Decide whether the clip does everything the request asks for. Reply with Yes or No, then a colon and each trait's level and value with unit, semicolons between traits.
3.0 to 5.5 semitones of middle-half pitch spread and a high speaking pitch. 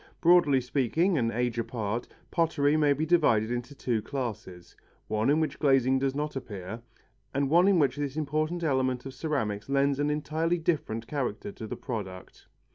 No: average, 4.6 semitones; low, 135 Hz